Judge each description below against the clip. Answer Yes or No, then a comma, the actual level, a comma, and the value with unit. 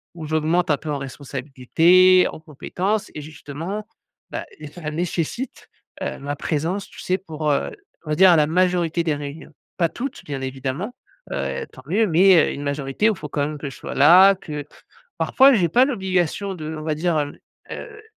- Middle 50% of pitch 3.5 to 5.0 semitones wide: Yes, average, 4.0 semitones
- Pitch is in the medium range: Yes, medium, 160 Hz